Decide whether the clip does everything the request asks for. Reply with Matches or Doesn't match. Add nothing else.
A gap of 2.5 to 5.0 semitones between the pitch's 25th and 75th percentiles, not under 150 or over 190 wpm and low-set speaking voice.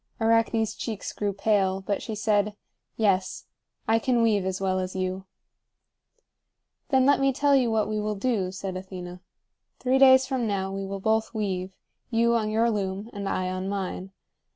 Doesn't match